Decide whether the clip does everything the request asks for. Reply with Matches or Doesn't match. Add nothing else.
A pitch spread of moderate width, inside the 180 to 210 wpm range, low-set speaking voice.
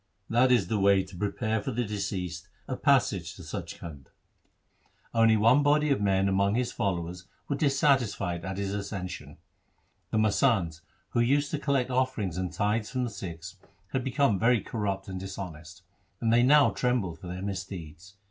Doesn't match